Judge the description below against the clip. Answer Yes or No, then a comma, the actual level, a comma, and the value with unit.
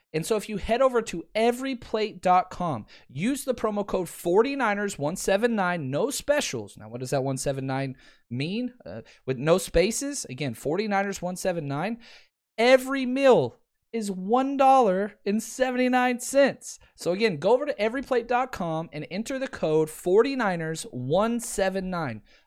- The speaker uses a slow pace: Yes, slow, 110 wpm